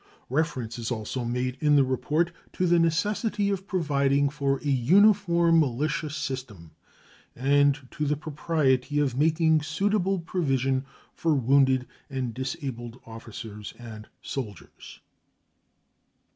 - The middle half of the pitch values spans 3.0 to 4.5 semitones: Yes, average, 4.2 semitones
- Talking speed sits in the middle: No, slow, 115 wpm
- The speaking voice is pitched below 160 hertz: Yes, medium, 140 Hz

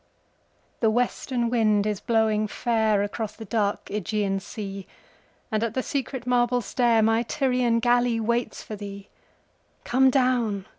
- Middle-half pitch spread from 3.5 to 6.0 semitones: No, narrow, 2.6 semitones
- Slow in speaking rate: Yes, slow, 115 wpm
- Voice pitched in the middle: No, high, 225 Hz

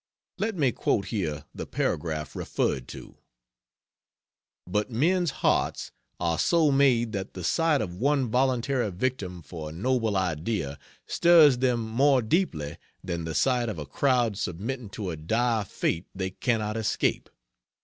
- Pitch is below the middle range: Yes, low, 110 Hz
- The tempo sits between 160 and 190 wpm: No, average, 145 wpm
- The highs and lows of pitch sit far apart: Yes, wide, 6.7 semitones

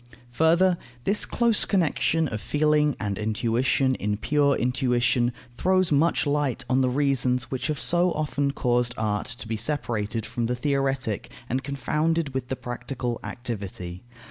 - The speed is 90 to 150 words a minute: Yes, average, 145 wpm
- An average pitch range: Yes, average, 3.8 semitones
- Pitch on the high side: No, low, 130 Hz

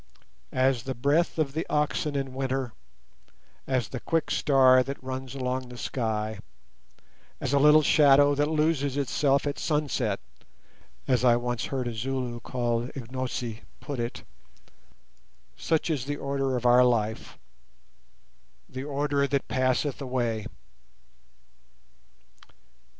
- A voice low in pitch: Yes, low, 130 Hz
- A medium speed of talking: No, slow, 125 wpm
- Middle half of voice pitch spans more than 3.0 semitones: No, narrow, 2.6 semitones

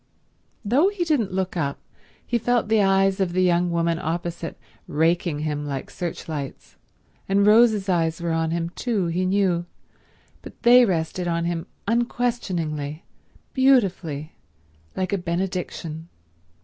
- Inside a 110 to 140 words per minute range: Yes, slow, 135 wpm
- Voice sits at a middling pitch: Yes, medium, 175 Hz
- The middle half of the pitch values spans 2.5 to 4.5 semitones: Yes, average, 3.6 semitones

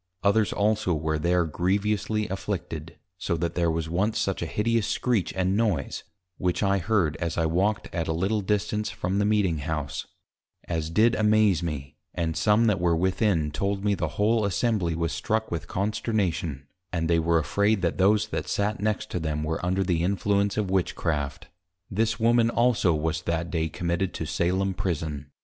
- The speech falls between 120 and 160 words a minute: No, average, 180 wpm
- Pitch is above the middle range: No, very low, 95 Hz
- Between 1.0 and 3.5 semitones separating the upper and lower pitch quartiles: No, average, 4.2 semitones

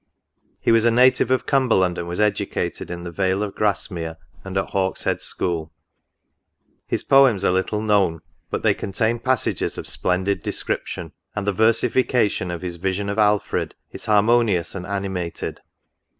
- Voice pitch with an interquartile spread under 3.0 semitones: No, average, 3.4 semitones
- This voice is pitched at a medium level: No, low, 100 Hz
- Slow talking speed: No, average, 165 wpm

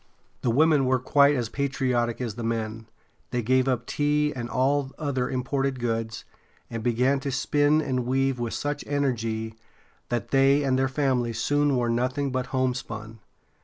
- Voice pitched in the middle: No, low, 130 Hz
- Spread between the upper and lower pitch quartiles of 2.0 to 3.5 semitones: Yes, average, 2.8 semitones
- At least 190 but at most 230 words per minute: No, average, 165 wpm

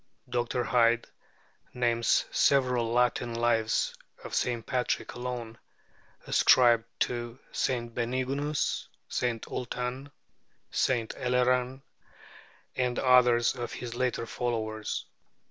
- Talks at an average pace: No, slow, 95 wpm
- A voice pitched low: Yes, low, 120 Hz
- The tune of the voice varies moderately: No, narrow, 1.3 semitones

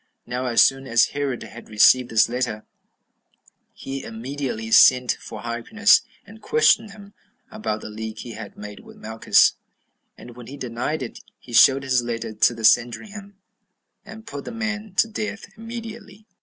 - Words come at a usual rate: Yes, average, 160 wpm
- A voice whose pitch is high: No, low, 130 Hz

